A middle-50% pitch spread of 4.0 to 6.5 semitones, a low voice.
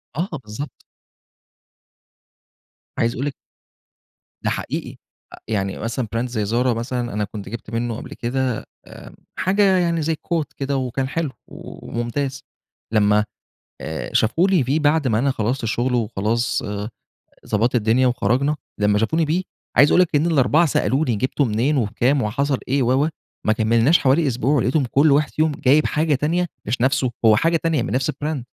Yes: average, 4.4 semitones; low, 130 Hz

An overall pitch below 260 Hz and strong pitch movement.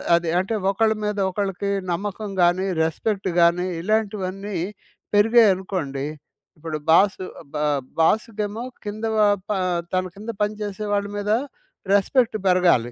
No: high, 200 Hz; narrow, 2.6 semitones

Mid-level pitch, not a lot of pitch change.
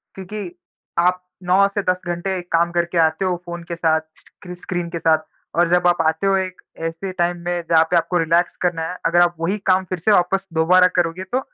Yes: medium, 175 Hz; narrow, 1.4 semitones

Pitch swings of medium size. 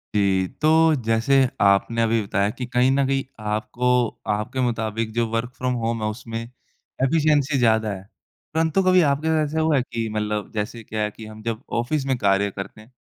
Yes: average, 3.8 semitones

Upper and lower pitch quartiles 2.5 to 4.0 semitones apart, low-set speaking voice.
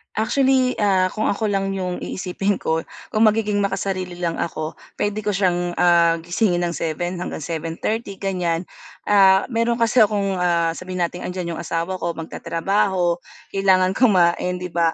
No: average, 2.9 semitones; medium, 185 Hz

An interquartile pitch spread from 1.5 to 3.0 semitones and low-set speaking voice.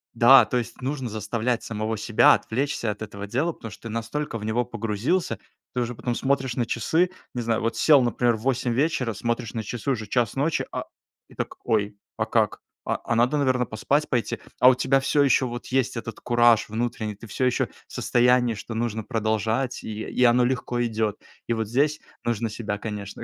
Yes: narrow, 2.6 semitones; low, 120 Hz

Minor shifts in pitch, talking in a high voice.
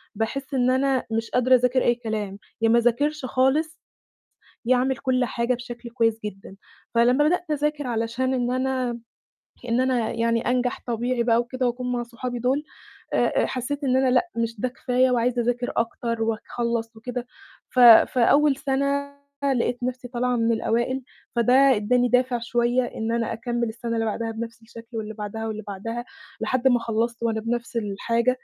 Yes: narrow, 1.9 semitones; high, 240 Hz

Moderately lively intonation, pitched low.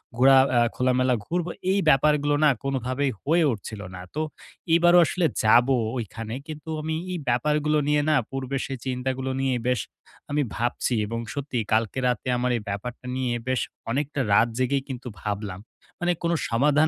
Yes: average, 3.5 semitones; low, 130 Hz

